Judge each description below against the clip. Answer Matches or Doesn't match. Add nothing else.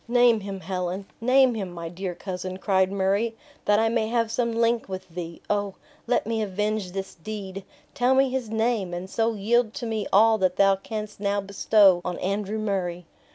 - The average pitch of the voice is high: Matches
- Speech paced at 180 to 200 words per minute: Matches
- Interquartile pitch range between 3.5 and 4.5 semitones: Doesn't match